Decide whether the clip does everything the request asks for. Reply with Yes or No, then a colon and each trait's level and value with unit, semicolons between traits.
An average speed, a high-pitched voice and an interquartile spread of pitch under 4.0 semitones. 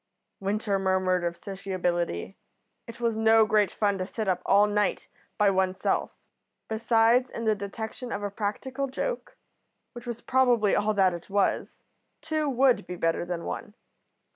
Yes: average, 160 wpm; high, 210 Hz; average, 3.5 semitones